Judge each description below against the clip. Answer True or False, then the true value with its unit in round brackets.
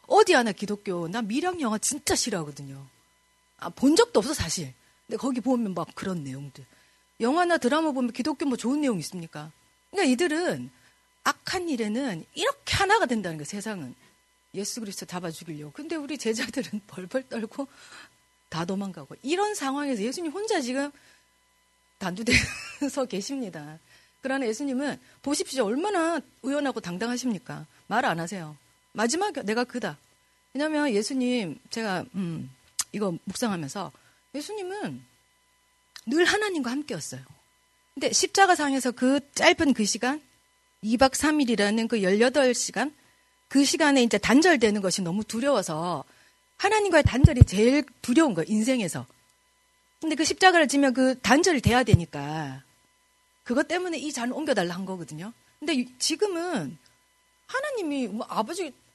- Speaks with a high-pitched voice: True (245 Hz)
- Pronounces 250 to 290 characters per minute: False (315 characters per minute)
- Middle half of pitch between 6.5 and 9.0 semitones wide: True (7.5 semitones)